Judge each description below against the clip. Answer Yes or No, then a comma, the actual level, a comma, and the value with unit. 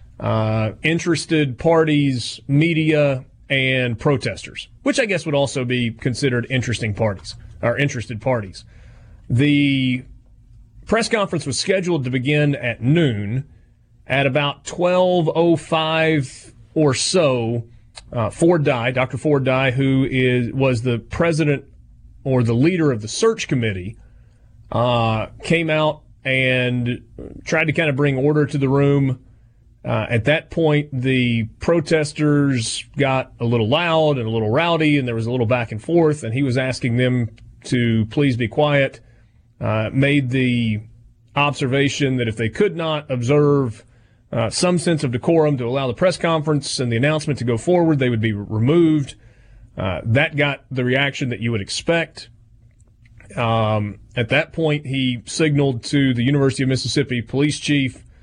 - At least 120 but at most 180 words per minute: Yes, average, 150 wpm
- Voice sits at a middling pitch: No, low, 130 Hz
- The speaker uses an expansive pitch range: No, average, 4.2 semitones